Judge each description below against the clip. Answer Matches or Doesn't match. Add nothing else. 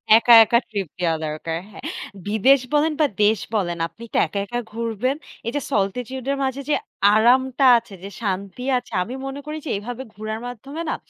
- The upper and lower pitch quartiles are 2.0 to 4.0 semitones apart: Doesn't match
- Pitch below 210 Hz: Doesn't match